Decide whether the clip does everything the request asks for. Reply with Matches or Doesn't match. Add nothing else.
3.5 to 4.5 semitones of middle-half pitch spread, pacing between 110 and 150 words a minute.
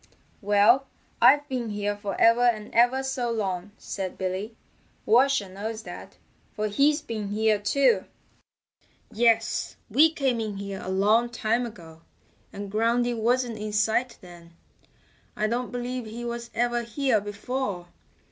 Doesn't match